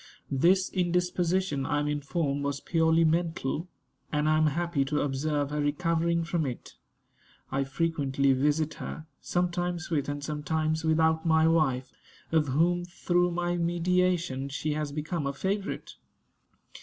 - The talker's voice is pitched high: No, medium, 160 Hz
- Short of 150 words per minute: Yes, average, 140 wpm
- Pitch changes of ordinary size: Yes, average, 3.0 semitones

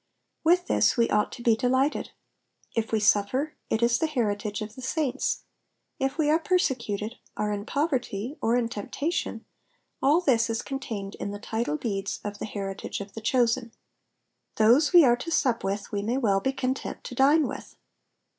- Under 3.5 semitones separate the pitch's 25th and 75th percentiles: No, average, 4.5 semitones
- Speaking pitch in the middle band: No, high, 235 Hz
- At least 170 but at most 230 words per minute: Yes, average, 180 wpm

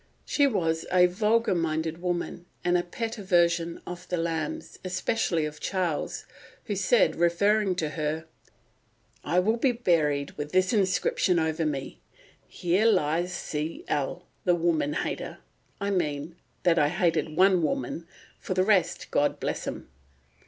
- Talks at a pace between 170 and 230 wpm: No, average, 140 wpm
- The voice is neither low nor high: Yes, medium, 175 Hz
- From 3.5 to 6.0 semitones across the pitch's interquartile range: No, average, 2.8 semitones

